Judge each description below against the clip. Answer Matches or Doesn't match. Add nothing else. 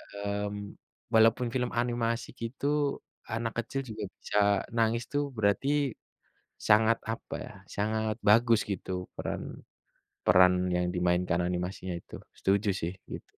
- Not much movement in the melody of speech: Doesn't match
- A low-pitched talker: Matches